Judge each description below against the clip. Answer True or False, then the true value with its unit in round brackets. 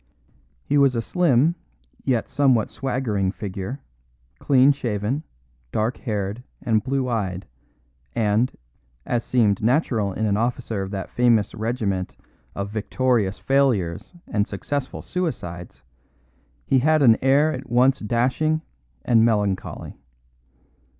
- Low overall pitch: True (115 Hz)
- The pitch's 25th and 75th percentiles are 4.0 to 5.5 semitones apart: True (4.4 semitones)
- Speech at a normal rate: False (115 wpm)